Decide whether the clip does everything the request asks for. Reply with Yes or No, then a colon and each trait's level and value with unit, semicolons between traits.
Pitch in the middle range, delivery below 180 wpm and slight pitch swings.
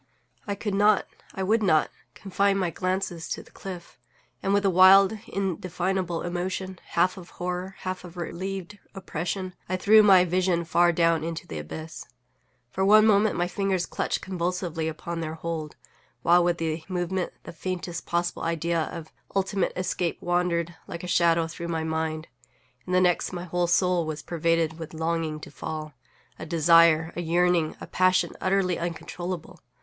Yes: medium, 175 Hz; average, 165 wpm; narrow, 2.1 semitones